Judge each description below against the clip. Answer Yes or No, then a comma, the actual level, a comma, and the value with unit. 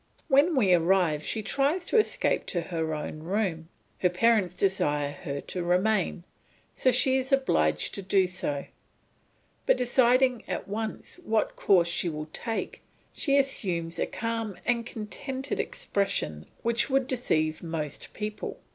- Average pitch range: No, wide, 6.7 semitones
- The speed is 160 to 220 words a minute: No, average, 145 wpm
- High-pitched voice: Yes, high, 200 Hz